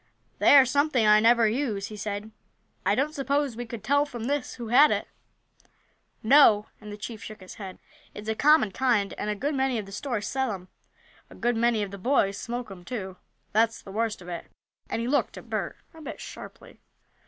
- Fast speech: Yes, fast, 210 wpm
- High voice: Yes, high, 225 Hz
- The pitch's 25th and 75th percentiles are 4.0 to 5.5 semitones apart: Yes, average, 4.3 semitones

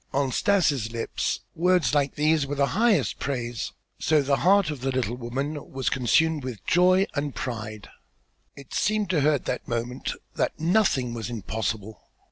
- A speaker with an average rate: Yes, average, 165 wpm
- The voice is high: No, medium, 140 Hz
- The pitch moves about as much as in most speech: Yes, average, 5.0 semitones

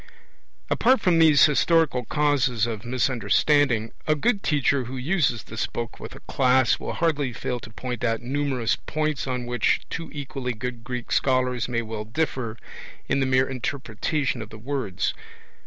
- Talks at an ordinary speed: Yes, average, 160 wpm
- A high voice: No, low, 130 Hz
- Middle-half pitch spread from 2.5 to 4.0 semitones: Yes, average, 3.5 semitones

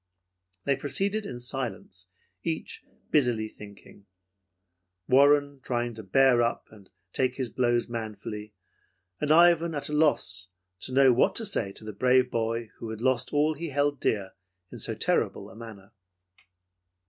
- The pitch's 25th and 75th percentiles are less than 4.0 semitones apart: No, average, 4.6 semitones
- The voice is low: Yes, low, 125 Hz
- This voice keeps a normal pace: Yes, average, 150 wpm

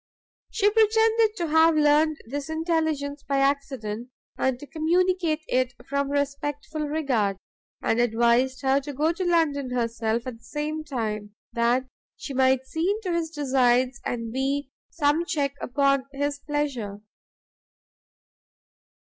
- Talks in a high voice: Yes, very high, 280 Hz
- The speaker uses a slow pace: Yes, slow, 130 wpm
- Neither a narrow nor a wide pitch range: Yes, average, 3.8 semitones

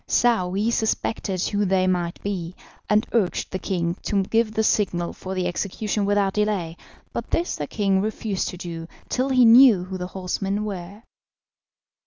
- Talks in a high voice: Yes, high, 195 Hz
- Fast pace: No, average, 165 wpm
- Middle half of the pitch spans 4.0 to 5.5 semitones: No, average, 2.9 semitones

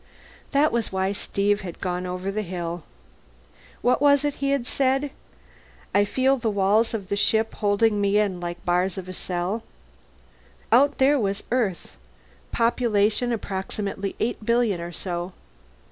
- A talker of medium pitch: No, high, 205 Hz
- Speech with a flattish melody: No, average, 4.1 semitones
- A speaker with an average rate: Yes, average, 155 wpm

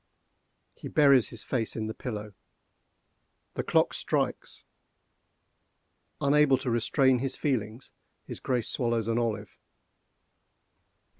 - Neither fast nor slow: No, slow, 105 wpm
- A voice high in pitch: No, low, 120 Hz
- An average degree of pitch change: Yes, average, 3.3 semitones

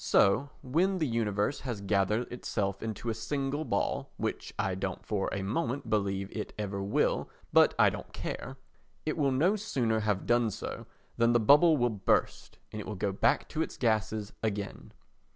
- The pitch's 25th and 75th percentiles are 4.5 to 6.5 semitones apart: Yes, average, 4.9 semitones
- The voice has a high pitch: No, low, 110 Hz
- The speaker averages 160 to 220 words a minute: Yes, average, 180 wpm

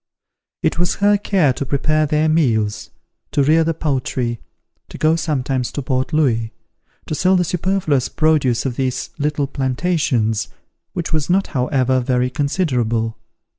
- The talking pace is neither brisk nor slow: Yes, average, 145 wpm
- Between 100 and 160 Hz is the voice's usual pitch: Yes, medium, 140 Hz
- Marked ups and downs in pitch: No, average, 4.1 semitones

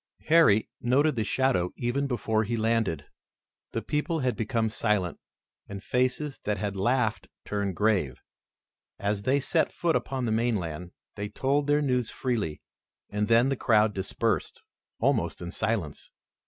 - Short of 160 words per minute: Yes, average, 145 wpm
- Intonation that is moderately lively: Yes, average, 4.4 semitones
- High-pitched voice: No, low, 110 Hz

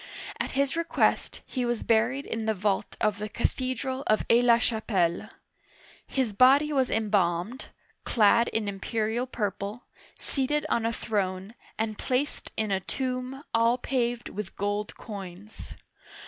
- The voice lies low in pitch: No, high, 230 Hz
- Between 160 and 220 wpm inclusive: No, average, 140 wpm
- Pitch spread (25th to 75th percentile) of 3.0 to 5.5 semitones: Yes, average, 3.6 semitones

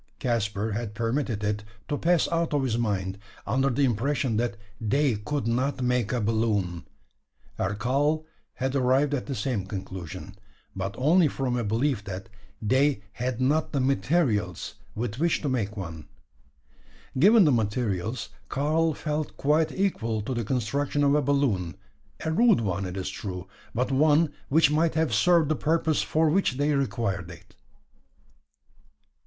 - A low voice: Yes, low, 125 Hz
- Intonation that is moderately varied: No, wide, 5.8 semitones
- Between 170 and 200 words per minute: No, average, 155 wpm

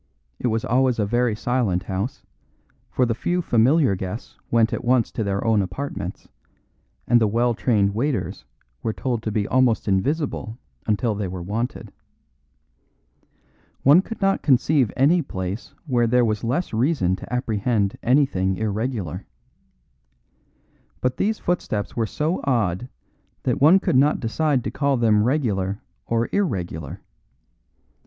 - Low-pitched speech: Yes, low, 115 Hz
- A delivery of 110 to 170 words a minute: Yes, average, 140 wpm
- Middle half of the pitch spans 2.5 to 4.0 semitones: No, average, 4.5 semitones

